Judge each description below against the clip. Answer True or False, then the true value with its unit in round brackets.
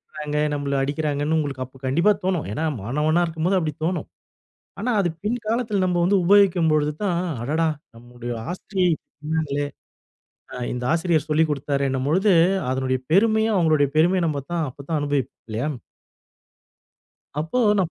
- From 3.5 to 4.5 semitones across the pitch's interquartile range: True (4.2 semitones)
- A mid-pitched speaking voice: True (155 Hz)